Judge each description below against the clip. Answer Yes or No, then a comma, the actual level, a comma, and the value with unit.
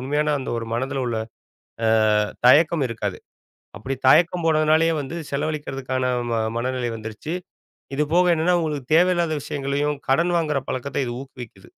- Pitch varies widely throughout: No, average, 3.7 semitones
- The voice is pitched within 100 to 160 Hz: Yes, medium, 140 Hz